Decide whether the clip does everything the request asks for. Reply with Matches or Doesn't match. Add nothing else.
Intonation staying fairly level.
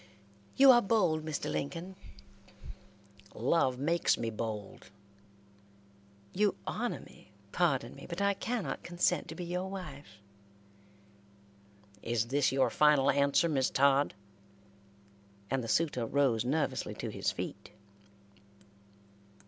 Doesn't match